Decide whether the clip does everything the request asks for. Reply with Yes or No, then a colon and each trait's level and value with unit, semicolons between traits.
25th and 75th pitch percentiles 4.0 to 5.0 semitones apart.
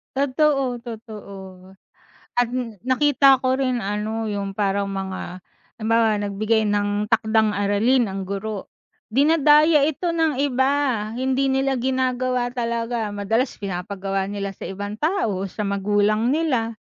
Yes: average, 4.5 semitones